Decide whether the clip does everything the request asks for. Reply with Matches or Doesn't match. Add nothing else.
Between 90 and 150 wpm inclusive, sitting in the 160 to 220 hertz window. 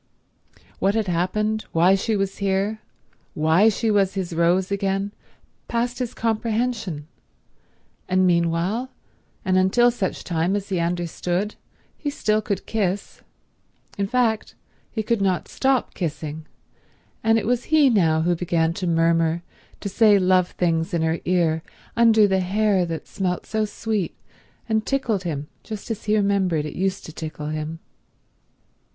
Matches